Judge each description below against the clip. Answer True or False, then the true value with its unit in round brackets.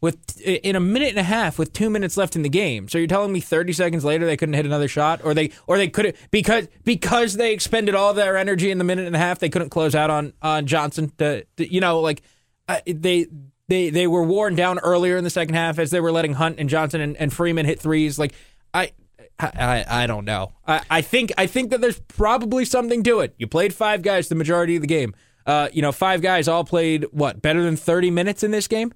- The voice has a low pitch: False (170 Hz)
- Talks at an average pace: False (250 wpm)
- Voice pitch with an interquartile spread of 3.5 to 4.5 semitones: True (3.9 semitones)